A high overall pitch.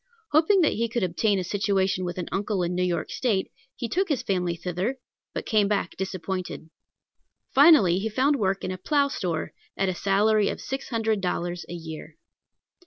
Yes: high, 195 Hz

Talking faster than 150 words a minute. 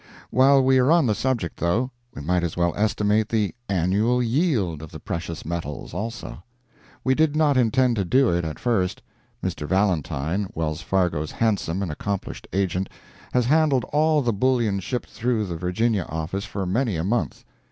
Yes: average, 175 wpm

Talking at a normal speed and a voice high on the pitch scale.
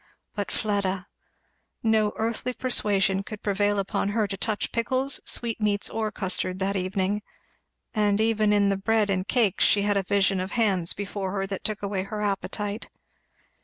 Yes: average, 165 wpm; high, 205 Hz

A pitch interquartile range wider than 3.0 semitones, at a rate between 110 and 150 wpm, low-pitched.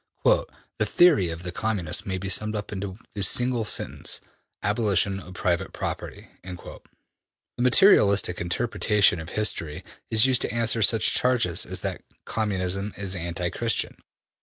Yes: average, 3.9 semitones; average, 140 wpm; low, 100 Hz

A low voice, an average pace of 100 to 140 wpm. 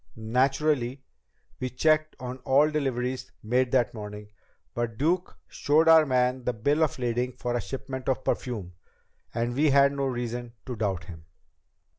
No: low, 125 Hz; average, 155 wpm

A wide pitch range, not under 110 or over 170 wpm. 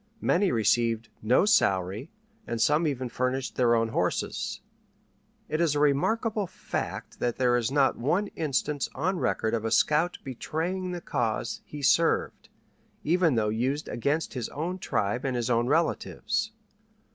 Yes: wide, 5.9 semitones; average, 150 wpm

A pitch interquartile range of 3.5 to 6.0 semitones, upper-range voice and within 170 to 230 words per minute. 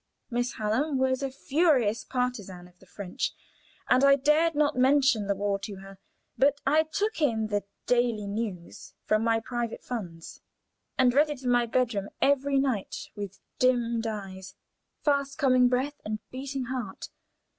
No: average, 4.7 semitones; high, 245 Hz; average, 155 wpm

